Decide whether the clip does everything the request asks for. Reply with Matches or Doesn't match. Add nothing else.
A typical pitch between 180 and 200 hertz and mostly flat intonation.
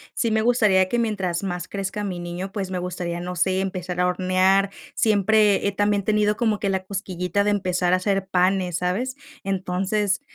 Matches